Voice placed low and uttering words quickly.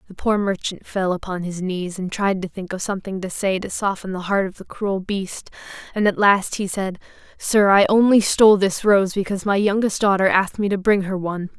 No: high, 195 Hz; fast, 230 wpm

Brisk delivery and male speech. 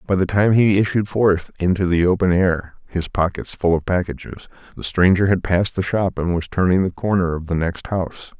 Yes: fast, 215 wpm; male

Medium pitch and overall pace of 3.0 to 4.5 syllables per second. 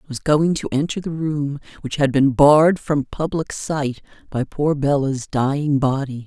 Yes: medium, 145 Hz; 4.4 syllables/s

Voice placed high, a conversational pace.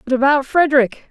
Yes: very high, 270 Hz; average, 165 wpm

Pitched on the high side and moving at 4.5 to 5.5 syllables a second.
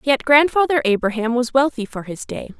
Yes: very high, 255 Hz; 5.3 syllables/s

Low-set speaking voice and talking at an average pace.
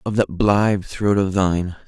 Yes: very low, 95 Hz; average, 190 wpm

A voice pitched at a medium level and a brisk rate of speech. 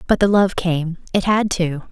Yes: medium, 180 Hz; fast, 220 wpm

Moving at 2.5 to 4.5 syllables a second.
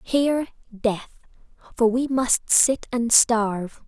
Yes: 3.5 syllables/s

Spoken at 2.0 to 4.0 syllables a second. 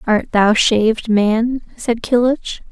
Yes: 3.5 syllables/s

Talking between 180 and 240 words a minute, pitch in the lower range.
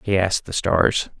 Yes: average, 200 wpm; very low, 95 Hz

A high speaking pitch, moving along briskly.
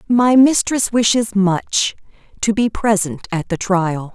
No: high, 210 Hz; average, 145 wpm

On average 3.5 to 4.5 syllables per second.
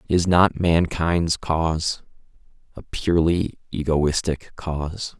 Yes: 3.6 syllables/s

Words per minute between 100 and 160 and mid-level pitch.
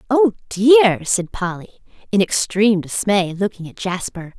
No: slow, 135 wpm; high, 200 Hz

